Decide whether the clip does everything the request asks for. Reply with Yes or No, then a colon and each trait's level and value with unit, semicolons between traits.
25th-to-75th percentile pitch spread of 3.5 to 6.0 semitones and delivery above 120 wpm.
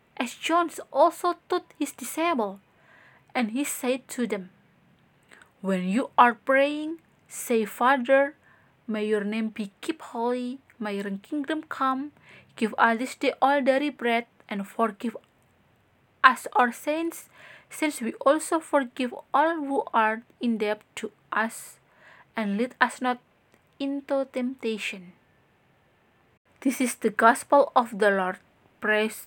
Yes: average, 4.2 semitones; average, 130 wpm